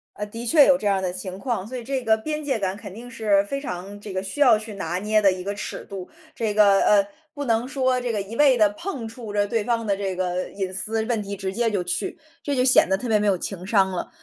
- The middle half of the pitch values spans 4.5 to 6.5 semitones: No, average, 3.8 semitones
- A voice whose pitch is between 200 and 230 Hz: Yes, high, 210 Hz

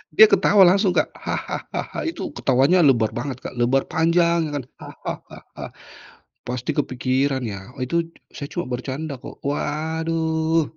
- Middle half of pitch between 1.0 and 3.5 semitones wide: No, average, 4.3 semitones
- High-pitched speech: No, medium, 150 Hz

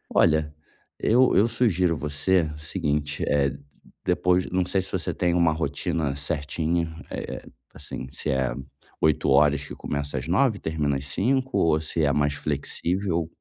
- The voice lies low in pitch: Yes, very low, 80 Hz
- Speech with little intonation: No, average, 3.8 semitones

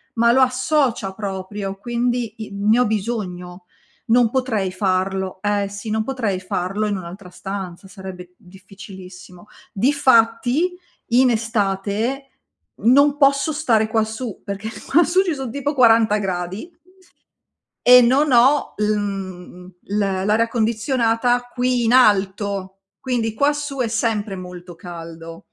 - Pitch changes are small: No, average, 4.4 semitones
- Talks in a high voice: Yes, high, 215 Hz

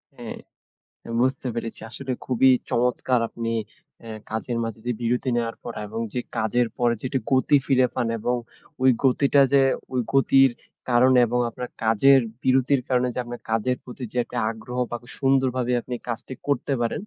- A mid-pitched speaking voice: No, low, 125 Hz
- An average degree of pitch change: No, narrow, 1.8 semitones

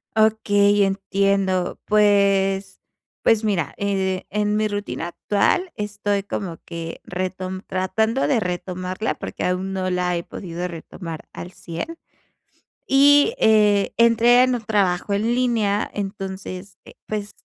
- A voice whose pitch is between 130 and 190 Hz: No, high, 200 Hz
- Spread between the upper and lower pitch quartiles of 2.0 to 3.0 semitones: Yes, narrow, 2.4 semitones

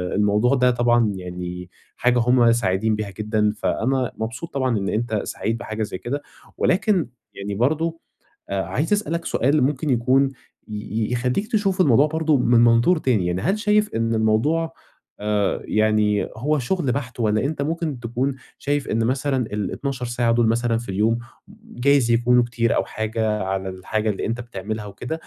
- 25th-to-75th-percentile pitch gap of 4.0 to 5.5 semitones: Yes, average, 4.4 semitones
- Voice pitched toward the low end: Yes, low, 120 Hz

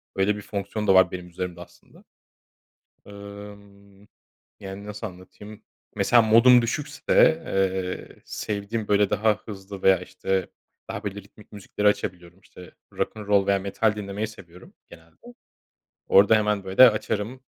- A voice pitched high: No, low, 100 Hz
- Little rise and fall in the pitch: Yes, narrow, 1.8 semitones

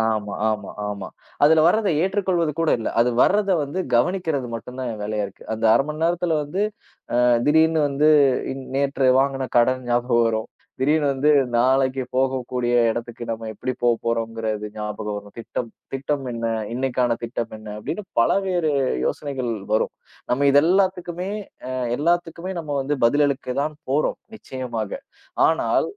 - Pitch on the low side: Yes, low, 130 Hz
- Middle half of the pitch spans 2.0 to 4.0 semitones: No, average, 5.1 semitones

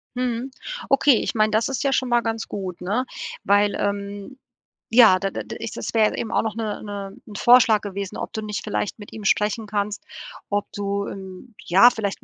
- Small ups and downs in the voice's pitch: Yes, narrow, 2.3 semitones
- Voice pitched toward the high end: Yes, high, 210 Hz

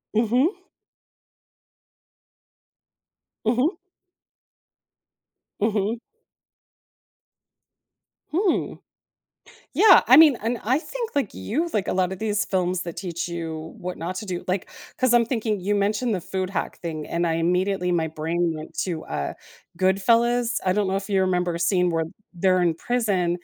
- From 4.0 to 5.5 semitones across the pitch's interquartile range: Yes, average, 4.8 semitones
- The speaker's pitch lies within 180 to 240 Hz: Yes, high, 190 Hz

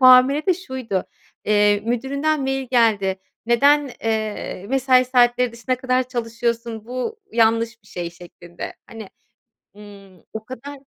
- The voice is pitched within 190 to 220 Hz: No, high, 235 Hz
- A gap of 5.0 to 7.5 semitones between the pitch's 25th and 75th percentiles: No, average, 3.2 semitones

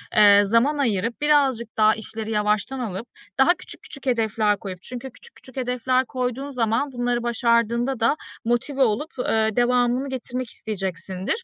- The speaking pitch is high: Yes, high, 240 Hz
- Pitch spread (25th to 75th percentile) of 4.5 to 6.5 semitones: No, average, 3.0 semitones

